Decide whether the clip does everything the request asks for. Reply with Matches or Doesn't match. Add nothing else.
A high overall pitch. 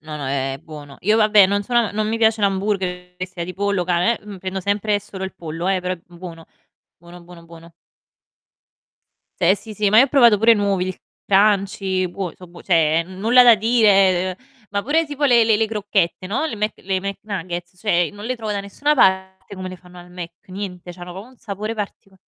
Matches